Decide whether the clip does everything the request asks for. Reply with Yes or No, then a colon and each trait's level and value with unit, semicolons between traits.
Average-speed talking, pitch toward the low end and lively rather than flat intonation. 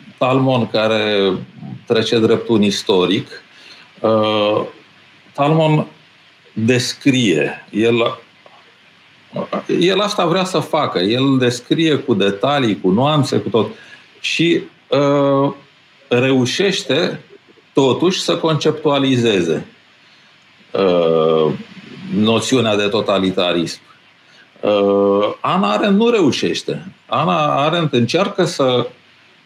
No: slow, 85 wpm; low, 125 Hz; wide, 6.1 semitones